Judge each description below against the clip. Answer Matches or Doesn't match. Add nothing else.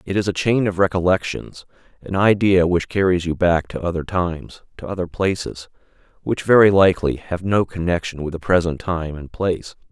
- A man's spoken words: Matches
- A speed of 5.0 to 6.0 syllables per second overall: Matches